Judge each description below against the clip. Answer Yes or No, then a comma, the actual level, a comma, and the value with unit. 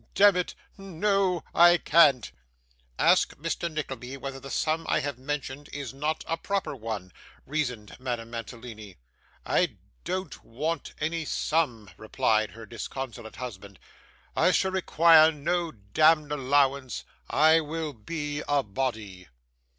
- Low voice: No, medium, 145 Hz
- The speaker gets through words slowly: Yes, slow, 125 wpm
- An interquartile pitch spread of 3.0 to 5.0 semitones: No, wide, 5.5 semitones